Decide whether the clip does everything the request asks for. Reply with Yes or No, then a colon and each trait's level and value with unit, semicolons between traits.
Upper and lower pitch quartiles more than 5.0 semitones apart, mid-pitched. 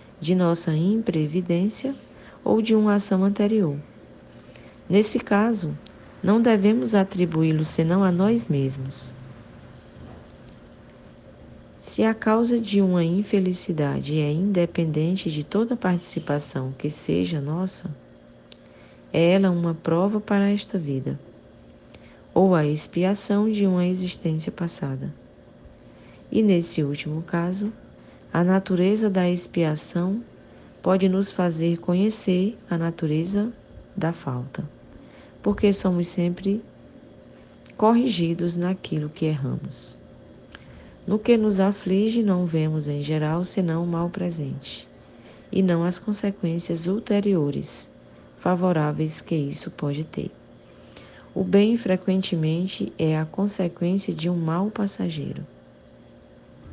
No: average, 4.7 semitones; medium, 175 Hz